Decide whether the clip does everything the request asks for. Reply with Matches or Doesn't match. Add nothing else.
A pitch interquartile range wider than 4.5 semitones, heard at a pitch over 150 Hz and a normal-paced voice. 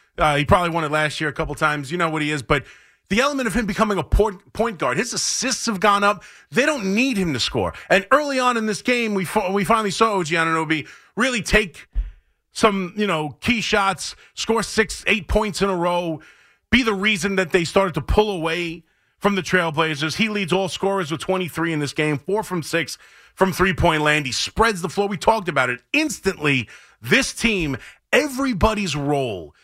Doesn't match